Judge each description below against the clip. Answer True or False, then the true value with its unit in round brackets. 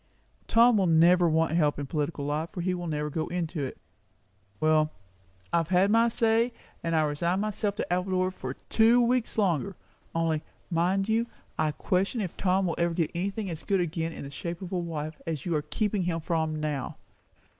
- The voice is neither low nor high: True (170 Hz)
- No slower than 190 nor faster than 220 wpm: True (195 wpm)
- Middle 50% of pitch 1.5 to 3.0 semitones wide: False (3.8 semitones)